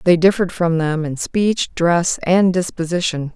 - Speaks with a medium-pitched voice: Yes, medium, 175 Hz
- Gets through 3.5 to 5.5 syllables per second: Yes, 4.4 syllables/s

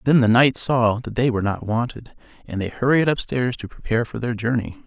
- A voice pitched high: No, low, 120 Hz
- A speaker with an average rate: No, fast, 220 wpm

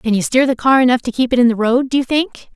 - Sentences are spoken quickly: Yes, fast, 355 wpm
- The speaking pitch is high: Yes, very high, 250 Hz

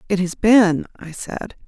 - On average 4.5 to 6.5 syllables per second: No, 3.8 syllables/s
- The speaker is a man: No, female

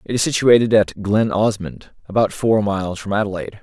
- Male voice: Yes, male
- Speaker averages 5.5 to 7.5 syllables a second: Yes, 5.6 syllables/s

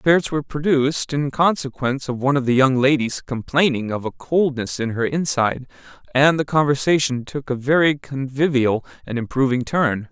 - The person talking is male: Yes, male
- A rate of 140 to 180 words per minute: Yes, average, 165 wpm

